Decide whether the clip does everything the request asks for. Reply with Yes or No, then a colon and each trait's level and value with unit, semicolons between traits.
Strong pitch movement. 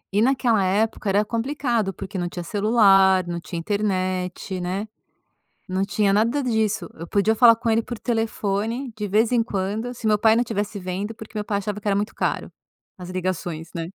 No: average, 3.0 semitones